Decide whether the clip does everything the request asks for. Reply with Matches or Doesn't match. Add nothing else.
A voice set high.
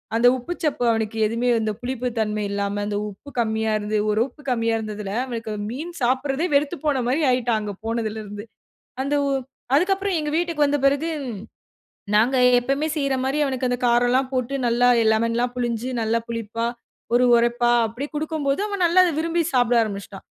Matches